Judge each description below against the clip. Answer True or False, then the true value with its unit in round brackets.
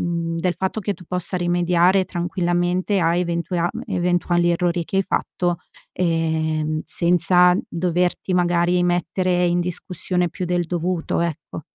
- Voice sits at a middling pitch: True (175 Hz)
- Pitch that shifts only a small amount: True (1.0 semitones)